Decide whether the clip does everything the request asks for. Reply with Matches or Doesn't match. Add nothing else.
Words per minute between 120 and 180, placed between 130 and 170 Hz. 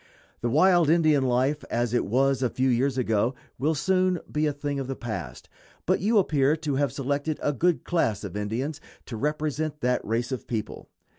Doesn't match